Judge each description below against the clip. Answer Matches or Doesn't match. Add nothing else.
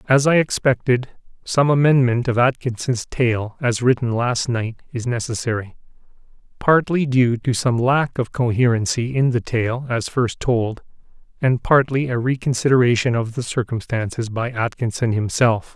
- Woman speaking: Doesn't match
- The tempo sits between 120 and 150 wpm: Matches